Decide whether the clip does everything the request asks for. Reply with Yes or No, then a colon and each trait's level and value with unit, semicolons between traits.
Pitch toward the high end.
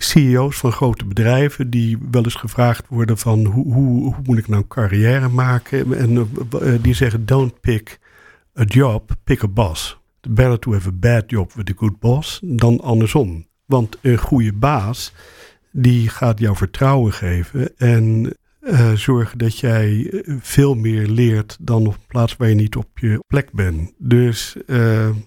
No: low, 120 Hz